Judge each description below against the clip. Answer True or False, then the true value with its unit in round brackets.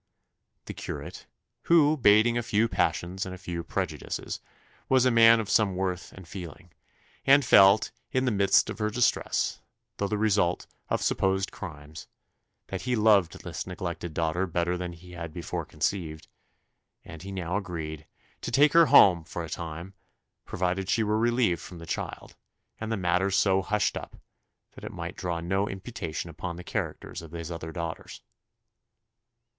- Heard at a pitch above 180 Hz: False (95 Hz)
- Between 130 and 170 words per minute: True (165 wpm)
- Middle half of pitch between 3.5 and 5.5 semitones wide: True (3.9 semitones)